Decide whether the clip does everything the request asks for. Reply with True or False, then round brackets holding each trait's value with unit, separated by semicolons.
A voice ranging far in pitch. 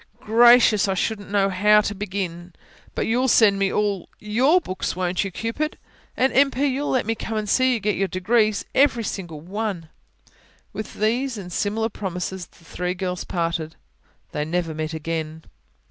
False (4.1 semitones)